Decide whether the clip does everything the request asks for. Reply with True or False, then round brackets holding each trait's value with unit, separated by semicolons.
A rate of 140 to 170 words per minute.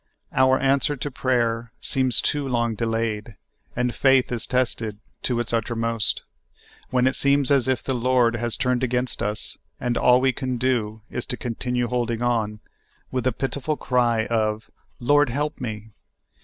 True (165 wpm)